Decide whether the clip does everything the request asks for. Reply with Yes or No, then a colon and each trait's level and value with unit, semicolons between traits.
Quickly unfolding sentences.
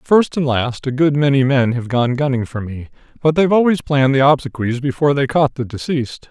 Yes: fast, 220 wpm